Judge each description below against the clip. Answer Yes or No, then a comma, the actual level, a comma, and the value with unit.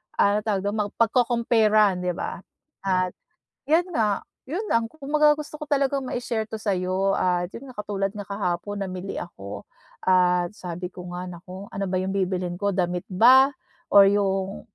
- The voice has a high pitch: Yes, high, 200 Hz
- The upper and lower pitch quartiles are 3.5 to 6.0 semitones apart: Yes, average, 4.0 semitones